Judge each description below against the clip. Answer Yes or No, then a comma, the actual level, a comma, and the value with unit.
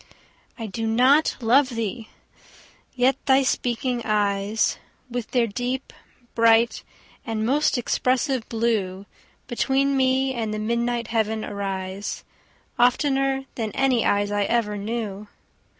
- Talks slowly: Yes, slow, 120 wpm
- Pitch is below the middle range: No, high, 235 Hz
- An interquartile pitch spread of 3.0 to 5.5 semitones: Yes, average, 3.4 semitones